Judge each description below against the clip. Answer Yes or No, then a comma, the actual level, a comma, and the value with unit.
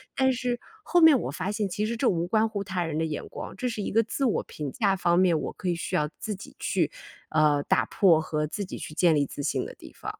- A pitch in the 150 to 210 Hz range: Yes, high, 190 Hz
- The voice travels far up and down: Yes, wide, 5.7 semitones